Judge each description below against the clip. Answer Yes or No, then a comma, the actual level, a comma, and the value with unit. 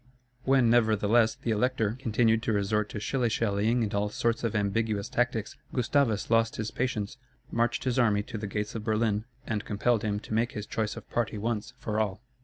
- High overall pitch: No, low, 110 Hz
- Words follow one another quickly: No, average, 195 wpm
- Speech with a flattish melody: Yes, narrow, 2.1 semitones